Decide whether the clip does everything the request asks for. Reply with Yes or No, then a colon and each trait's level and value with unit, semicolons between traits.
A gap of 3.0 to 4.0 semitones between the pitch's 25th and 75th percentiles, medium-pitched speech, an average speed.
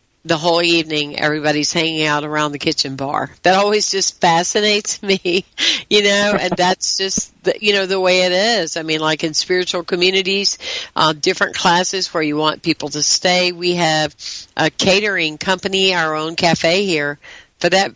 Yes: average, 3.4 semitones; medium, 180 Hz; average, 175 wpm